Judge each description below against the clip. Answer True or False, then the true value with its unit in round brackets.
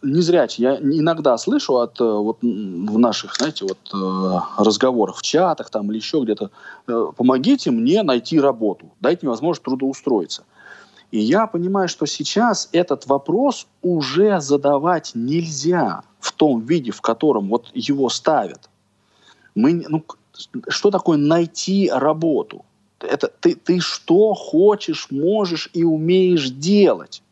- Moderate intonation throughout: False (6.9 semitones)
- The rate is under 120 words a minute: False (130 wpm)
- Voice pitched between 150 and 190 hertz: True (165 Hz)